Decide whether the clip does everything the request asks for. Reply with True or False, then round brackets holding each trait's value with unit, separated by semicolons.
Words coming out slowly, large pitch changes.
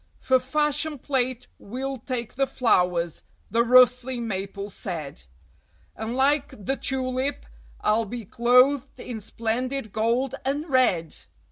False (120 wpm; 3.4 semitones)